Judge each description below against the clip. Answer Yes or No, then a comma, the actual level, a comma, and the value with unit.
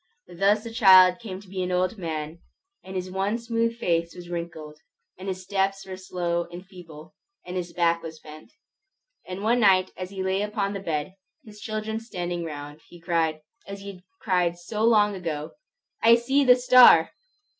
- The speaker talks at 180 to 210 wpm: Yes, average, 185 wpm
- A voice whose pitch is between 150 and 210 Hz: Yes, medium, 185 Hz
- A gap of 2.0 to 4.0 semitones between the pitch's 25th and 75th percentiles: Yes, average, 3.4 semitones